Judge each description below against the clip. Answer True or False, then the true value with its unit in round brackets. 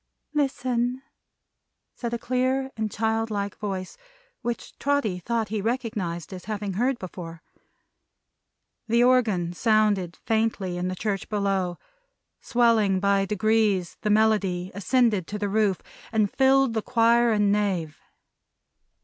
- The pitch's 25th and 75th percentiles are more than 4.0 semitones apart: False (3.4 semitones)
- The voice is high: True (215 Hz)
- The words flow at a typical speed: False (125 wpm)